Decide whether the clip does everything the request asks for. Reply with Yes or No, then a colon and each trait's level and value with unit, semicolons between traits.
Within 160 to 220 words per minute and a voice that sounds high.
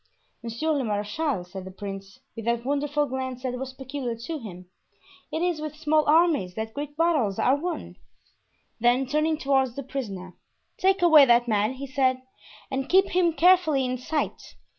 Yes: average, 170 wpm; very high, 265 Hz